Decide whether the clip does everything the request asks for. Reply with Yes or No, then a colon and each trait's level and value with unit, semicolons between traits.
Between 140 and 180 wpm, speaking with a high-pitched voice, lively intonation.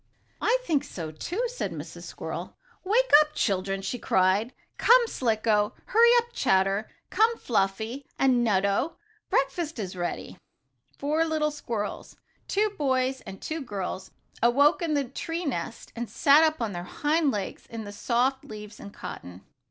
Yes: average, 150 wpm; very high, 250 Hz; wide, 7.5 semitones